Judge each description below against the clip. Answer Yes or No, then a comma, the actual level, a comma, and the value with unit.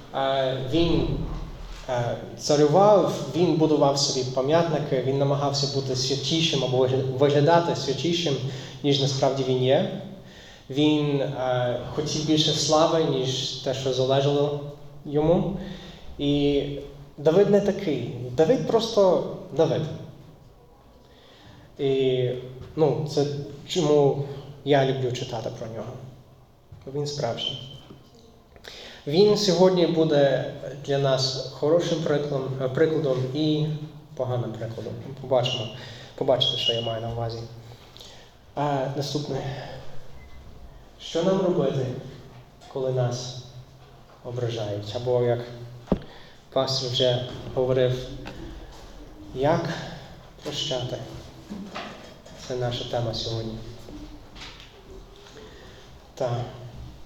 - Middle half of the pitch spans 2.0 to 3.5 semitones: Yes, average, 3.1 semitones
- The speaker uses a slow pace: Yes, slow, 85 wpm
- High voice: No, low, 135 Hz